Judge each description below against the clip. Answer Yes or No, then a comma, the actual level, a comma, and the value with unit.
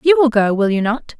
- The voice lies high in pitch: Yes, high, 245 Hz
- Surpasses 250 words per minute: Yes, fast, 300 wpm